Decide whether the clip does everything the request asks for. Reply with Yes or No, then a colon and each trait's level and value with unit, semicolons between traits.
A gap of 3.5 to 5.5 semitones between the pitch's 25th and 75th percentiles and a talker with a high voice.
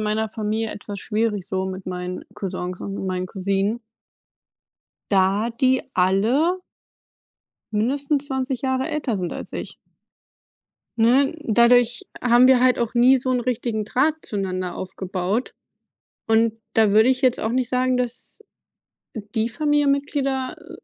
Yes: average, 4.4 semitones; high, 230 Hz